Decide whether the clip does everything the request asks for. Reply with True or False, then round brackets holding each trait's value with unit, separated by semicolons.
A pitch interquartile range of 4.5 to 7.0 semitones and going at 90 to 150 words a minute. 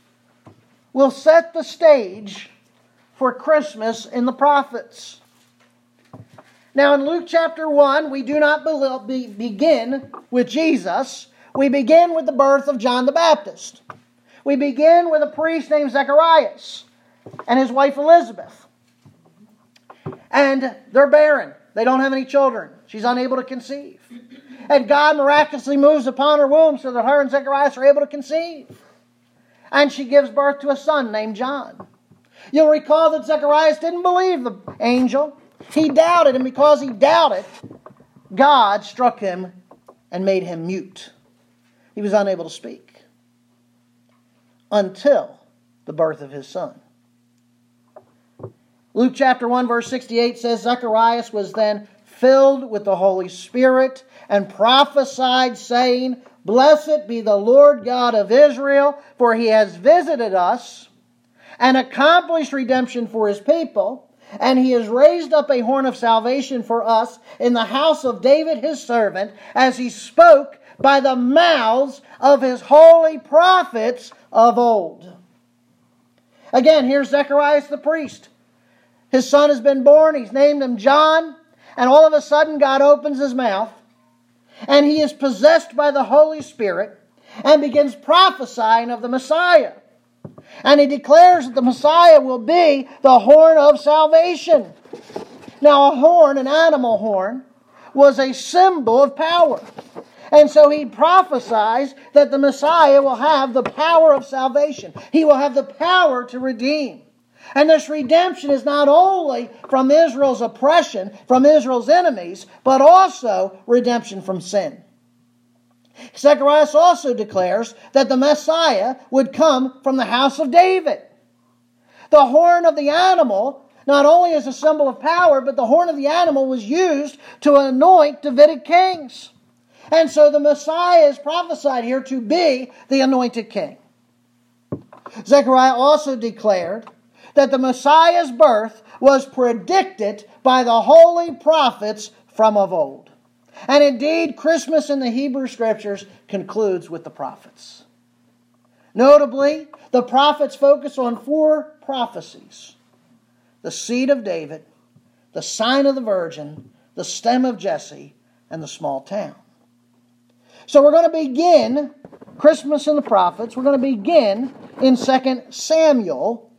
True (4.8 semitones; 140 wpm)